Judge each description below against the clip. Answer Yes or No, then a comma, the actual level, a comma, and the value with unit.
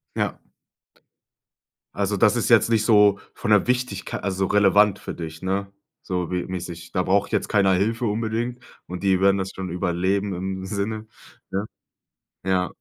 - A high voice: No, very low, 95 Hz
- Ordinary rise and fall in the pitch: No, narrow, 2.1 semitones